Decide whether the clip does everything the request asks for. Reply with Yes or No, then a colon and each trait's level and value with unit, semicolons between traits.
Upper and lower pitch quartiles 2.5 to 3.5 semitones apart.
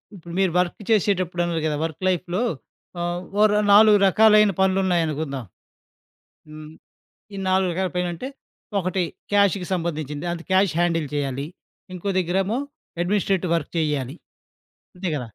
Yes: average, 2.8 semitones